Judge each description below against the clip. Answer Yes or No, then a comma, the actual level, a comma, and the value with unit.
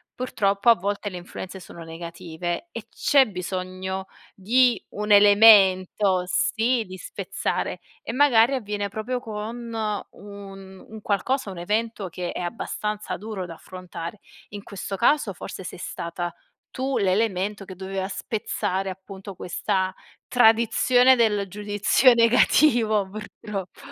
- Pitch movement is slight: No, average, 3.1 semitones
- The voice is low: No, high, 200 Hz